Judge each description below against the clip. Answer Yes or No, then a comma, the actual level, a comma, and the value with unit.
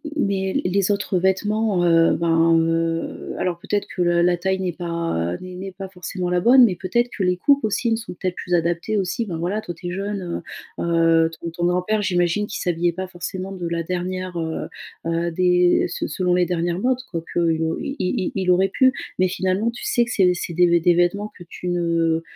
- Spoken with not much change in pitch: Yes, narrow, 2.2 semitones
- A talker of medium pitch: Yes, medium, 180 Hz